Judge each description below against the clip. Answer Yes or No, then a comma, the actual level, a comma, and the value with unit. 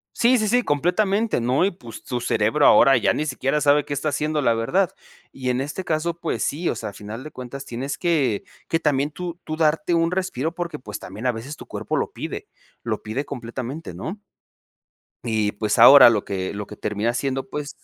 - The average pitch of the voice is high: No, medium, 140 Hz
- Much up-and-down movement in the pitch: Yes, wide, 5.7 semitones